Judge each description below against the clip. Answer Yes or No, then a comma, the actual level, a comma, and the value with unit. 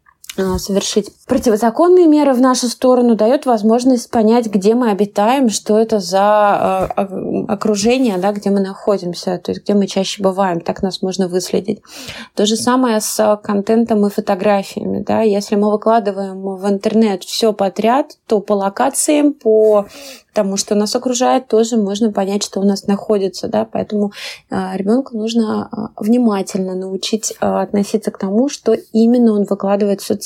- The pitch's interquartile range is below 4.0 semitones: Yes, narrow, 2.6 semitones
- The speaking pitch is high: Yes, high, 215 Hz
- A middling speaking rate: Yes, average, 150 wpm